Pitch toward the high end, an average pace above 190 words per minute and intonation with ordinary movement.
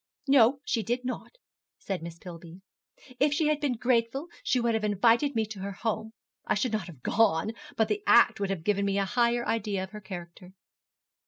Yes: high, 220 Hz; average, 200 wpm; average, 3.9 semitones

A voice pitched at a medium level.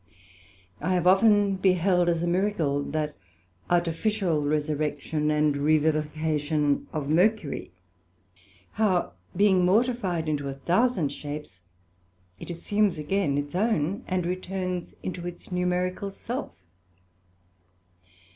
Yes: medium, 175 Hz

